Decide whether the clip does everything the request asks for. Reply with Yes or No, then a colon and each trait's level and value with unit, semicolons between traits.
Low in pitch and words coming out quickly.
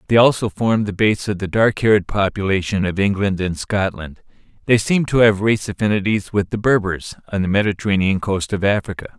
No: low, 100 Hz; average, 190 wpm